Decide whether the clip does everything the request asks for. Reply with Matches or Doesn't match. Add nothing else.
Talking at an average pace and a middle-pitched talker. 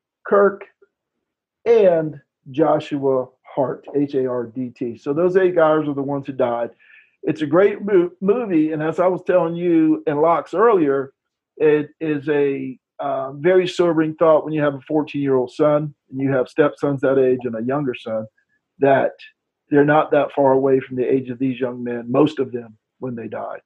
Matches